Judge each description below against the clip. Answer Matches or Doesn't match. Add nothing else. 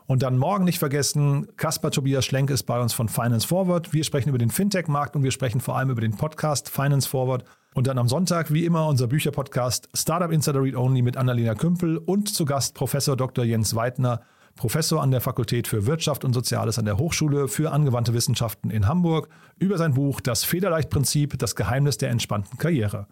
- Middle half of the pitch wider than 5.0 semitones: Doesn't match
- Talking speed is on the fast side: Matches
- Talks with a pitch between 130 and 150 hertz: Matches